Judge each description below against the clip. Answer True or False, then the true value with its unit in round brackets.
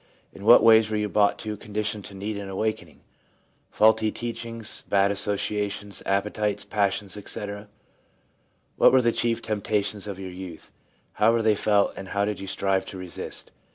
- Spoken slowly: False (175 wpm)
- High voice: False (105 Hz)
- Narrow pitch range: True (1.5 semitones)